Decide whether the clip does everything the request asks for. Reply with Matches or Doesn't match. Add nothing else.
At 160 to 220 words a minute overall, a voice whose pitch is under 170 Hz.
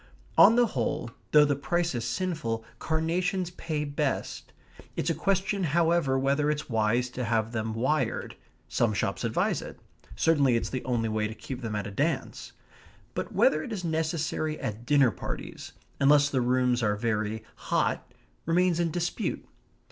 Matches